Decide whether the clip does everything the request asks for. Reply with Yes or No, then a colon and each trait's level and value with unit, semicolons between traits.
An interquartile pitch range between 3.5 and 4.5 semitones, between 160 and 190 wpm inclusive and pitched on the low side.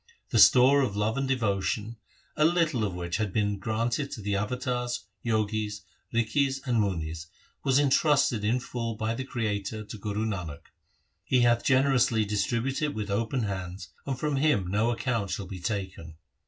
Yes: average, 4.1 semitones; average, 170 wpm; low, 110 Hz